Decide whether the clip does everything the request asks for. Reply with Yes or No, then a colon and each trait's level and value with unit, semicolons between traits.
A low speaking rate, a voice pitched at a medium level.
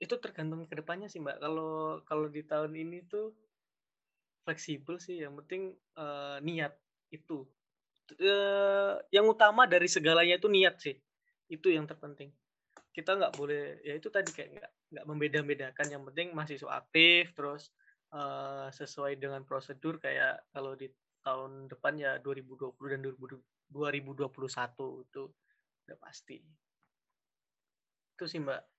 No: average, 135 wpm; medium, 155 Hz